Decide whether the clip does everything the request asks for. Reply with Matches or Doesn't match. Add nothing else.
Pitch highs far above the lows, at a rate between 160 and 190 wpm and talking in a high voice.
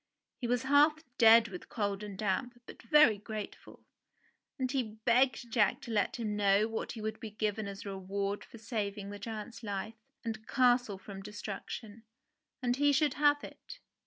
Doesn't match